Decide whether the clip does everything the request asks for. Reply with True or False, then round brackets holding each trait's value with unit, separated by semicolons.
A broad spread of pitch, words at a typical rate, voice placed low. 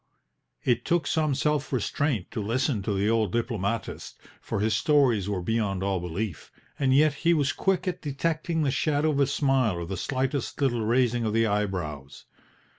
True (5.9 semitones; 180 wpm; 120 Hz)